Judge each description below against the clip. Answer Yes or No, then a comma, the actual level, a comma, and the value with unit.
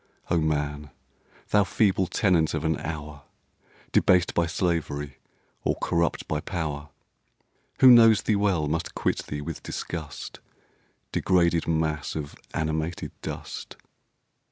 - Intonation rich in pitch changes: No, average, 2.9 semitones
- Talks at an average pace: No, slow, 120 wpm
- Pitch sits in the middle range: No, very low, 80 Hz